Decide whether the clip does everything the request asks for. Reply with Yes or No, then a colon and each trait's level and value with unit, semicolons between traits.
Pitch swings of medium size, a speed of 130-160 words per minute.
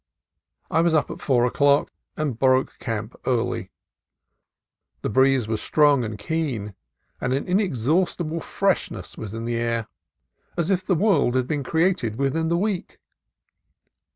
No: wide, 5.8 semitones; average, 150 wpm